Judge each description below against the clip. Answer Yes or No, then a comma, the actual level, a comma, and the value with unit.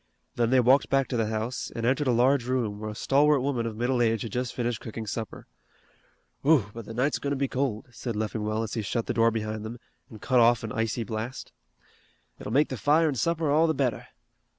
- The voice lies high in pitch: No, low, 120 Hz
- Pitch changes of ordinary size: Yes, average, 3.3 semitones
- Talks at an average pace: No, fast, 230 wpm